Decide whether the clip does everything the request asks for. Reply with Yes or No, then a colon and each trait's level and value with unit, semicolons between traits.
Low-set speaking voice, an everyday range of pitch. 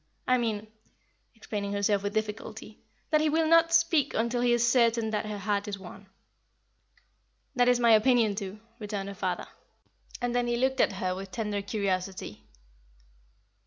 No: high, 220 Hz; average, 3.3 semitones